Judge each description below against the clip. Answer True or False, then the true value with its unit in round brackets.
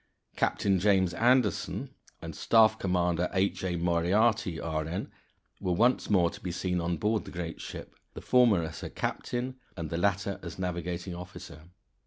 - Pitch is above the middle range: False (90 Hz)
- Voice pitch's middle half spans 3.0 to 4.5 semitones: True (3.3 semitones)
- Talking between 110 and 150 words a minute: False (160 wpm)